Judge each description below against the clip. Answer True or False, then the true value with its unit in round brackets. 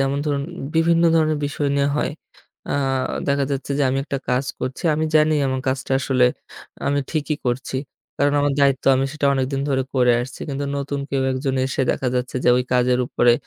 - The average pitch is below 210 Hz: True (135 Hz)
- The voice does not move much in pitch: True (1.7 semitones)